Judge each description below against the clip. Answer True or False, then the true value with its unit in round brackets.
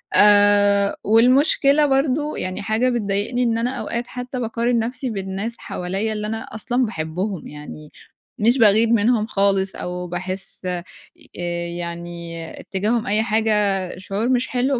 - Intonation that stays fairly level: False (4.1 semitones)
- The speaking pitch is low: False (210 Hz)